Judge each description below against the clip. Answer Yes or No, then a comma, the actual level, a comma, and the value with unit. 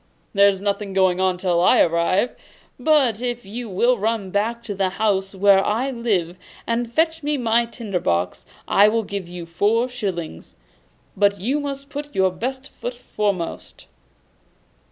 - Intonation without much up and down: No, average, 4.3 semitones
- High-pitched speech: Yes, high, 205 Hz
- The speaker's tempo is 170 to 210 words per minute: No, average, 155 wpm